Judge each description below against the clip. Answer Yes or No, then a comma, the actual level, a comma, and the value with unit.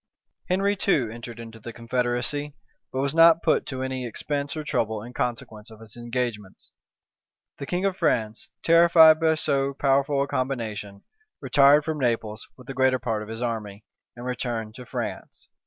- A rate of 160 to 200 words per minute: Yes, average, 170 wpm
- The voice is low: Yes, low, 125 Hz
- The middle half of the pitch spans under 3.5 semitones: No, average, 4.2 semitones